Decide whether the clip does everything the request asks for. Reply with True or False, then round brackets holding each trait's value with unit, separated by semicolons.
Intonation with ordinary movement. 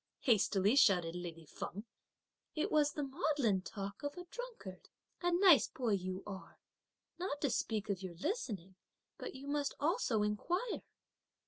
False (7.8 semitones)